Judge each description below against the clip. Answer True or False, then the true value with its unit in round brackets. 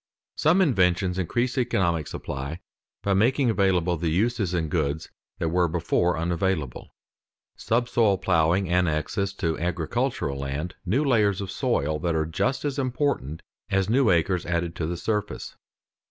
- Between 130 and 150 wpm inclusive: True (145 wpm)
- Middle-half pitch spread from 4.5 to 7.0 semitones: True (5.2 semitones)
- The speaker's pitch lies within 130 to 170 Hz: False (90 Hz)